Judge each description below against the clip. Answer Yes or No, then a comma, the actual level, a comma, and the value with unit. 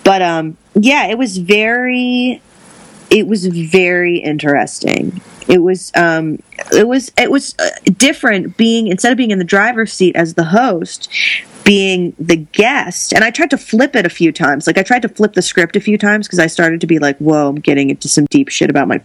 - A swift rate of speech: Yes, fast, 210 wpm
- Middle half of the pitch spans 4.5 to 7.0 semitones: Yes, wide, 5.6 semitones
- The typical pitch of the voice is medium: No, high, 195 Hz